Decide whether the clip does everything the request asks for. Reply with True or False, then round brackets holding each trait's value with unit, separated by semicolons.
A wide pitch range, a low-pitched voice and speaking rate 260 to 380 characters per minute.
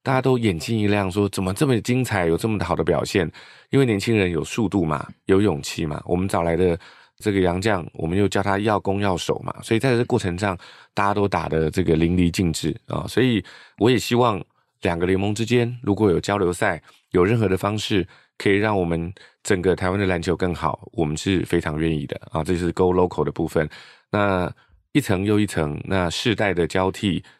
False (3.7 semitones; 95 Hz; 320 characters per minute)